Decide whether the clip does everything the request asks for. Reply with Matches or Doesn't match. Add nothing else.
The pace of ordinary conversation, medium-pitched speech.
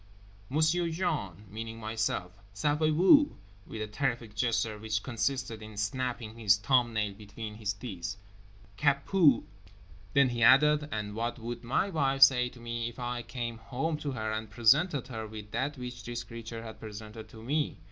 Doesn't match